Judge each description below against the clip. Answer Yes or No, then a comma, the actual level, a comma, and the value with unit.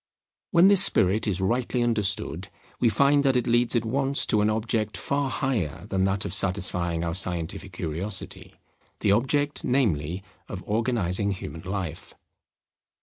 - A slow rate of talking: No, average, 145 wpm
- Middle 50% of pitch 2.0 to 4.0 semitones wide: No, average, 5.2 semitones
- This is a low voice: Yes, low, 105 Hz